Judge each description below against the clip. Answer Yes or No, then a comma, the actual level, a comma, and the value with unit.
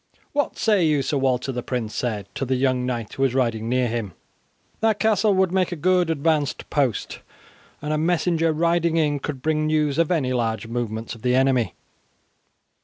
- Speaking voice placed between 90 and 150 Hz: Yes, medium, 140 Hz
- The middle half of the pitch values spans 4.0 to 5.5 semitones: Yes, average, 4.9 semitones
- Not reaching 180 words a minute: No, average, 185 wpm